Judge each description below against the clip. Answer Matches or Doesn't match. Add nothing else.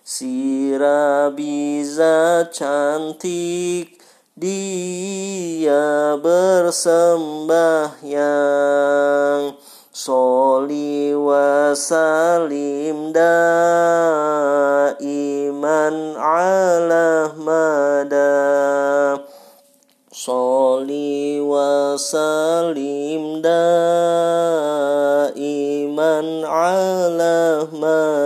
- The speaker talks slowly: Matches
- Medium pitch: Matches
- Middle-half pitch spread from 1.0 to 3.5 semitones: Matches